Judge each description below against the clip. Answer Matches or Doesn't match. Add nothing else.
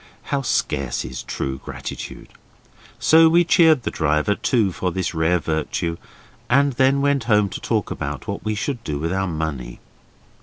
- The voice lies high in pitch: Doesn't match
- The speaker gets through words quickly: Doesn't match